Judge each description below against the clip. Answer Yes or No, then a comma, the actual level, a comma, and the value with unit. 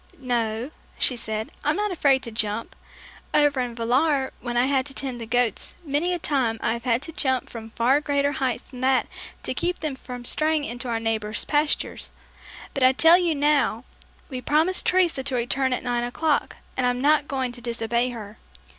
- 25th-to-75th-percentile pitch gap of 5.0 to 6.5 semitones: No, average, 3.6 semitones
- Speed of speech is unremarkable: Yes, average, 195 wpm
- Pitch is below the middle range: No, very high, 260 Hz